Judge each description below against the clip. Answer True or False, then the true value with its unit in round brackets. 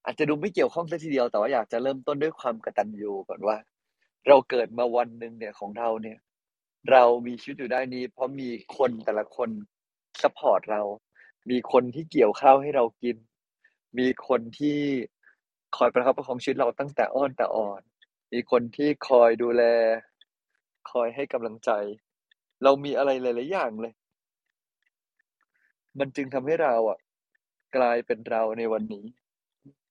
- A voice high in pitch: False (120 Hz)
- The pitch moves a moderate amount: True (3.2 semitones)